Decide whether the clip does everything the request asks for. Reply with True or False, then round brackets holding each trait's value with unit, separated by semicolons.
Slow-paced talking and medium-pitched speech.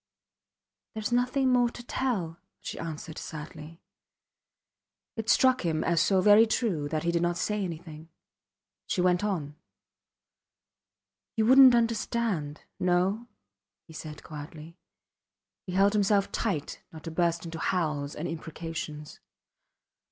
True (130 wpm; 175 Hz)